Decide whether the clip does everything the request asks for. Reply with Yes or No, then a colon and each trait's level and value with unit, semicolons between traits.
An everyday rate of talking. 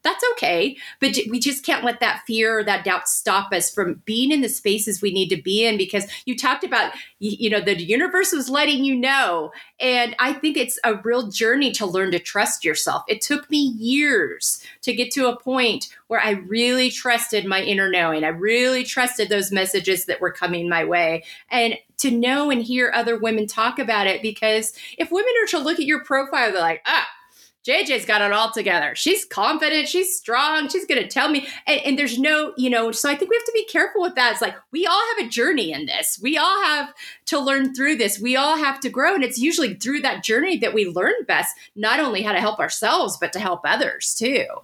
No: fast, 225 wpm